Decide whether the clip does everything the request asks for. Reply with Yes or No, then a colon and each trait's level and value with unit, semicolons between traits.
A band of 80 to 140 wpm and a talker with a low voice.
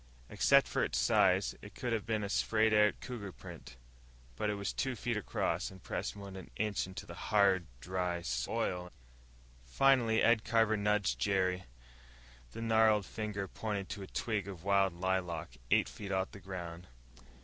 No: average, 170 wpm; low, 100 Hz